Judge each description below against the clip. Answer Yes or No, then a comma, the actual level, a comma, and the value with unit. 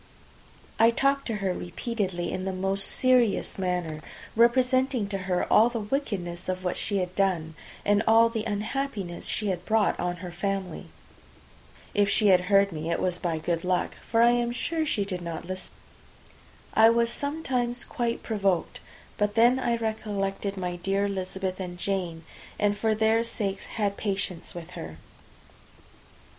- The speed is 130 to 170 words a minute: Yes, average, 155 wpm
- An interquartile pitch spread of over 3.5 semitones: Yes, average, 4.0 semitones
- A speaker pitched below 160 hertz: No, high, 200 Hz